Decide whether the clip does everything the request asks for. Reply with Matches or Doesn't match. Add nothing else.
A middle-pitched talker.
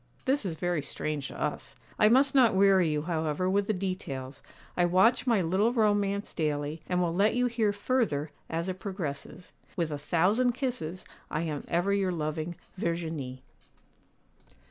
Matches